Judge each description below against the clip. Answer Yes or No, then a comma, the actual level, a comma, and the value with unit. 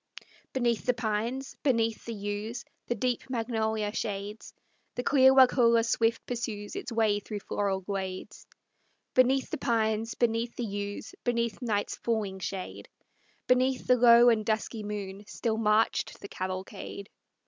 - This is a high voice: Yes, high, 225 Hz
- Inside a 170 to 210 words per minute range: No, slow, 135 wpm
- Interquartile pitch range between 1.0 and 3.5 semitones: Yes, average, 2.7 semitones